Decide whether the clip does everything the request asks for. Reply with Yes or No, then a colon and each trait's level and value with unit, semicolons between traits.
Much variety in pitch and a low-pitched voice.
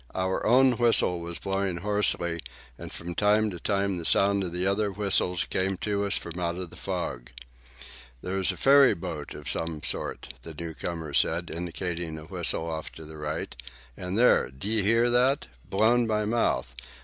No: average, 3.7 semitones; very low, 95 Hz